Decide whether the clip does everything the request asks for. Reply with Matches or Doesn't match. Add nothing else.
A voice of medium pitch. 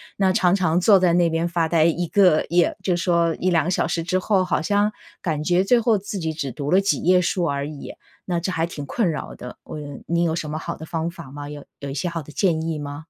Matches